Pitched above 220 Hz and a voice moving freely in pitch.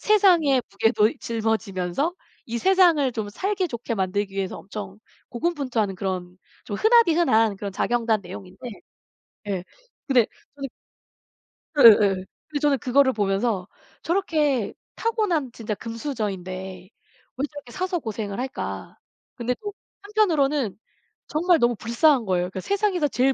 Yes: high, 240 Hz; wide, 7.0 semitones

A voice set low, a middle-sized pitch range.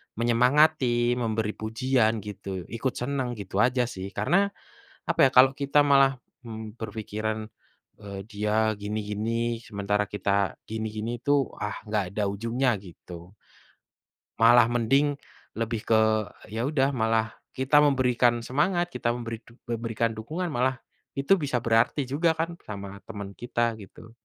Yes: low, 115 Hz; average, 3.6 semitones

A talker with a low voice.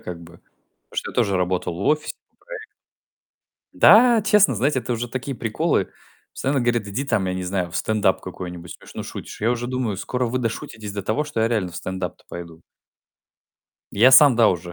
Yes: low, 110 Hz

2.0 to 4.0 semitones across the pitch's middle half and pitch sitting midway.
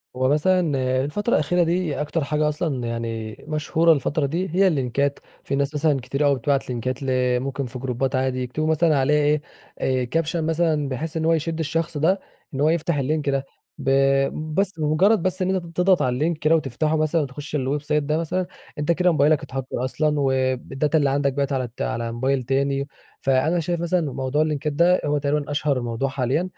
Yes: average, 3.3 semitones; medium, 150 Hz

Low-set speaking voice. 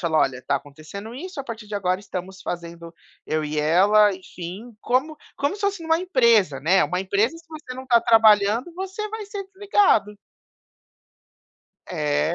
No: high, 210 Hz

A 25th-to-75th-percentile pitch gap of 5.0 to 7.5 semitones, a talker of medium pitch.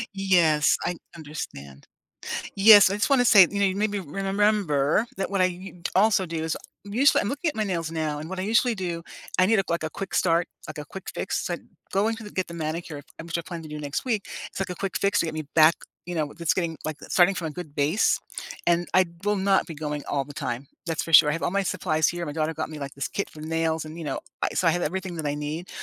No: average, 3.9 semitones; medium, 170 Hz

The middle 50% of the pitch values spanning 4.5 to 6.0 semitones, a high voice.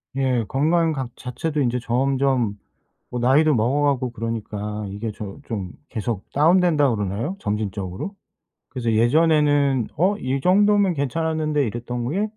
No: average, 5.1 semitones; low, 130 Hz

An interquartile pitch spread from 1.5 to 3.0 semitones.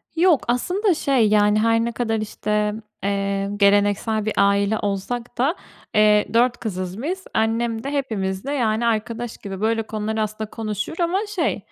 Yes: average, 2.7 semitones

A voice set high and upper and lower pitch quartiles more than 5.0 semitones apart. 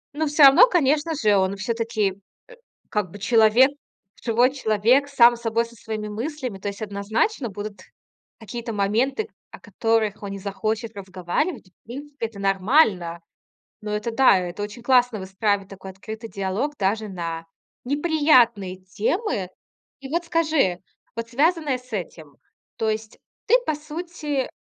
Yes: high, 225 Hz; wide, 5.4 semitones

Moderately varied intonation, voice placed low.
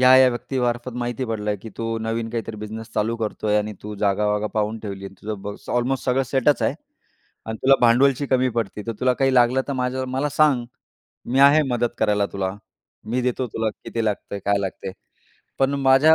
Yes: average, 3.5 semitones; low, 115 Hz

